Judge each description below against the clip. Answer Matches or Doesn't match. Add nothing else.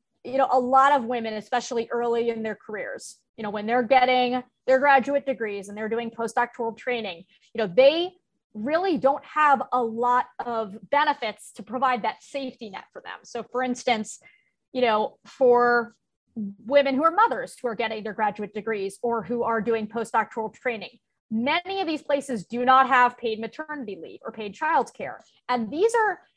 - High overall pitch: Matches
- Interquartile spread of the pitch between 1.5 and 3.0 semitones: Doesn't match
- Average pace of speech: Matches